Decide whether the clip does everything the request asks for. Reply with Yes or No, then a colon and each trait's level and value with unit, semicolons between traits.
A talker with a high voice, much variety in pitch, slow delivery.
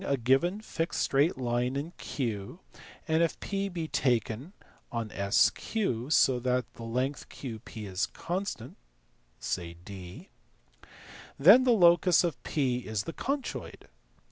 No: low, 135 Hz; wide, 6.8 semitones; slow, 130 wpm